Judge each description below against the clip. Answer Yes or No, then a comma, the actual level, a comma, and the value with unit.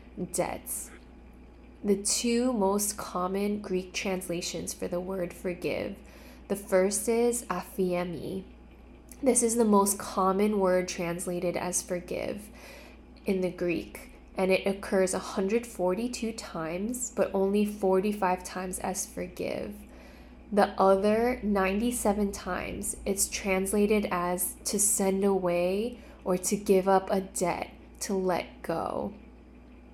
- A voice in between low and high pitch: No, high, 195 Hz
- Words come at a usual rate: No, slow, 115 wpm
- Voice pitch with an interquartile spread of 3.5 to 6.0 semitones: No, narrow, 2.4 semitones